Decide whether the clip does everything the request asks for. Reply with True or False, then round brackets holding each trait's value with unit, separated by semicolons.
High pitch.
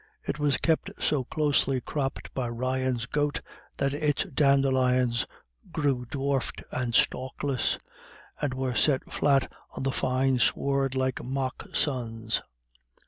False (130 Hz)